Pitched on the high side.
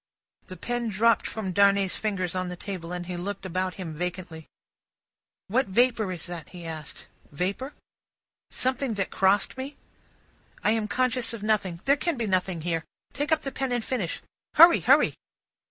Yes: high, 200 Hz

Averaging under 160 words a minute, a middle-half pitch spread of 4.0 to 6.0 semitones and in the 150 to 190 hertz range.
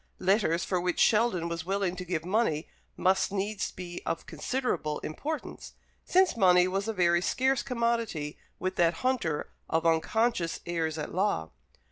Yes: average, 150 wpm; average, 5.1 semitones; medium, 185 Hz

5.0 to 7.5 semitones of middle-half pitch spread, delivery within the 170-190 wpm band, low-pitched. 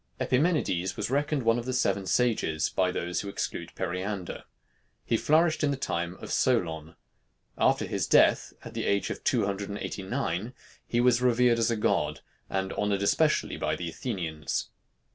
Yes: average, 5.3 semitones; average, 175 wpm; low, 105 Hz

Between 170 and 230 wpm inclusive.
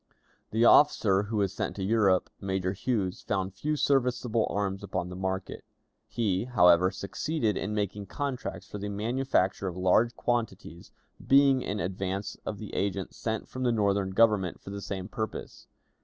No: average, 160 wpm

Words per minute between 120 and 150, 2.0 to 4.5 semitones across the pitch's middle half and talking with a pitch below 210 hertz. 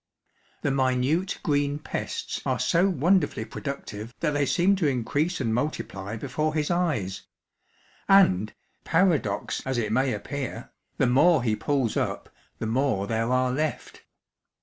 No: average, 140 wpm; average, 5.0 semitones; low, 135 Hz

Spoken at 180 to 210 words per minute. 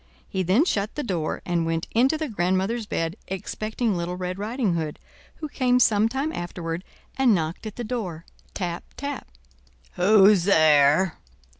No: average, 150 wpm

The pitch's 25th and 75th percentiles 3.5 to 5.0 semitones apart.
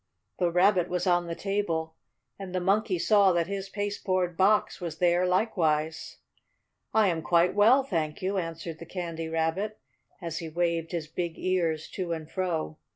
No: average, 2.8 semitones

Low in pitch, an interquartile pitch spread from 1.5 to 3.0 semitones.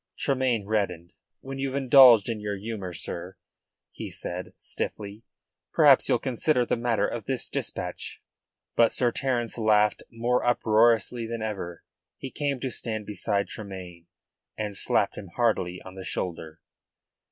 No: low, 110 Hz; average, 3.6 semitones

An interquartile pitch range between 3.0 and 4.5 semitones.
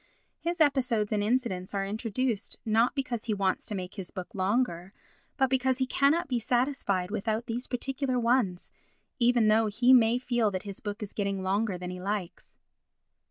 Yes: average, 4.1 semitones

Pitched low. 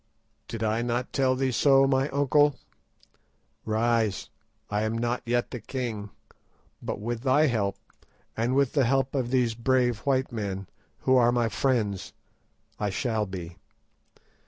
Yes: low, 120 Hz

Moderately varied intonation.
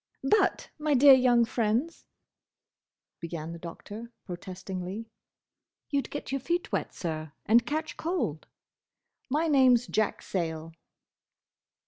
No: wide, 8.0 semitones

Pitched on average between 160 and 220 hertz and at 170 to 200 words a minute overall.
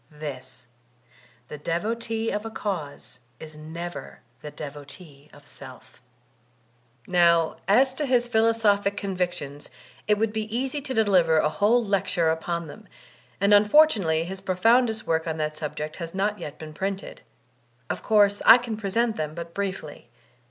No: high, 190 Hz; average, 150 wpm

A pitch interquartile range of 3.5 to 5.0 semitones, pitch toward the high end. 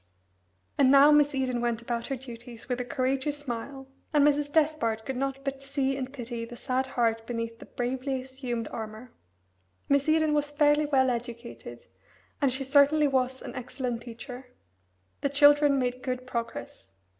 No: average, 2.8 semitones; very high, 260 Hz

